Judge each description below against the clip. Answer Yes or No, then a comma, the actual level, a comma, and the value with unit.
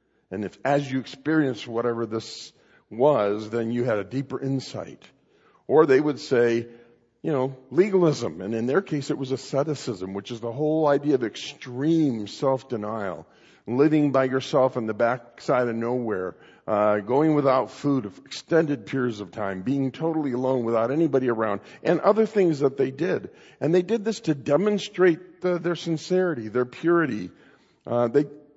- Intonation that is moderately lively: Yes, average, 4.5 semitones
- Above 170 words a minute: No, average, 165 wpm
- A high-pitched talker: No, low, 135 Hz